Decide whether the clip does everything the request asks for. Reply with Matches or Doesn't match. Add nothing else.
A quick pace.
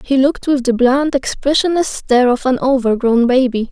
Doesn't match